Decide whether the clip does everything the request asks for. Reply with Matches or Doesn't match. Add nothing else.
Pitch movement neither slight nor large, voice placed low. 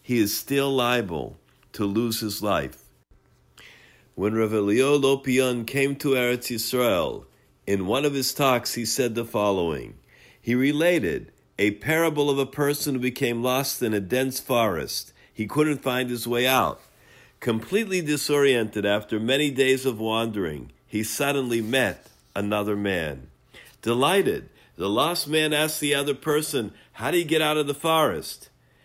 Matches